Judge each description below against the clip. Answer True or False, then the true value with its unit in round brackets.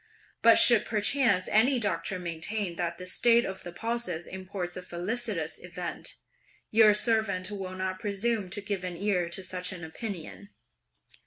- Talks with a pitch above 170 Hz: True (190 Hz)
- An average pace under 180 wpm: True (155 wpm)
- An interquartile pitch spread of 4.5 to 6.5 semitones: False (3.3 semitones)